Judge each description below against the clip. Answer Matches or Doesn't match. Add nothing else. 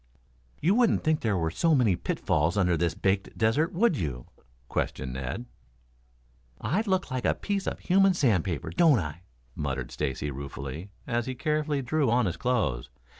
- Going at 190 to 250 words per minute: Doesn't match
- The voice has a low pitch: Matches